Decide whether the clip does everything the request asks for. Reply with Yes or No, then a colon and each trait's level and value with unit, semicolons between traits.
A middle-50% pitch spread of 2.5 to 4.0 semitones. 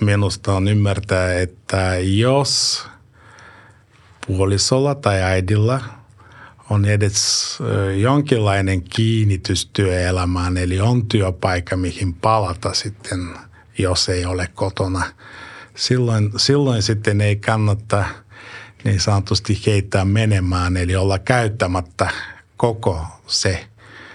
Yes: average, 2.9 semitones